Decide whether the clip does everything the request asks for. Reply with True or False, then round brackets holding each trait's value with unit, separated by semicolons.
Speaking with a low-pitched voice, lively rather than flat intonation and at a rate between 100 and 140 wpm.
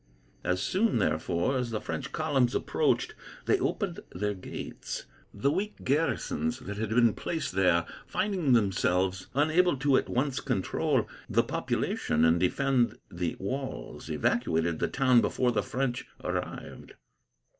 True (120 Hz; 6.9 semitones; 135 wpm)